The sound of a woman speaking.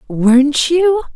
Yes: female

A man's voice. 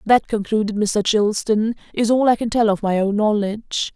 No: female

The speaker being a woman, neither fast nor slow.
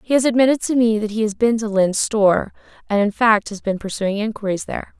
No: female; fast, 240 wpm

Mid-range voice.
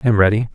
No: low, 110 Hz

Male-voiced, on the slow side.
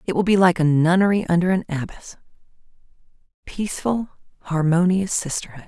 No: female; slow, 125 wpm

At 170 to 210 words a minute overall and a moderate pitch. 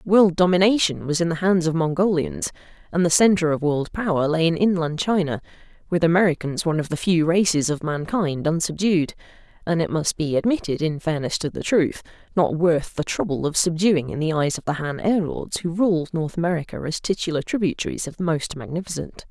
Yes: average, 190 wpm; medium, 165 Hz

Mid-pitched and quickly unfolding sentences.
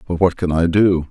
No: very low, 90 Hz; fast, 270 wpm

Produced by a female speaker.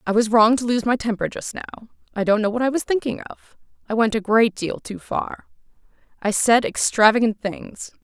Yes: female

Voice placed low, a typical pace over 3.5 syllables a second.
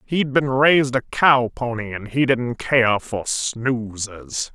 No: low, 125 Hz; 3.4 syllables/s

